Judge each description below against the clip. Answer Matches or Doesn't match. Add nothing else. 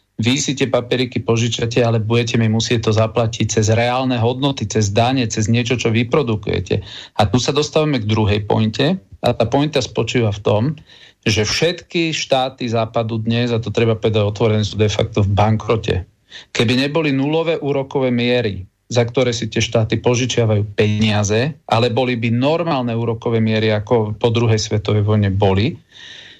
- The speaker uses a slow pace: Doesn't match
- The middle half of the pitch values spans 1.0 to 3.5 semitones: Matches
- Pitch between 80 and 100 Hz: Doesn't match